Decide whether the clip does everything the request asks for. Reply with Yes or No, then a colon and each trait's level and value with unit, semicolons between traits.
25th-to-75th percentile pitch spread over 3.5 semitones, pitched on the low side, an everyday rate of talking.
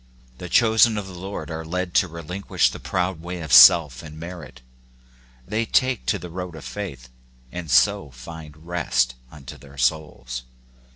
Yes: average, 4.0 semitones; very low, 85 Hz; average, 165 wpm